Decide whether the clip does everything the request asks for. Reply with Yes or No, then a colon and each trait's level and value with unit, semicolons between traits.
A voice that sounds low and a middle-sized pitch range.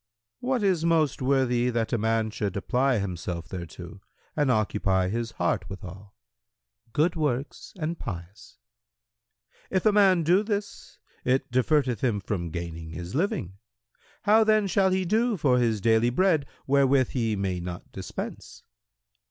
No: low, 120 Hz; wide, 8.9 semitones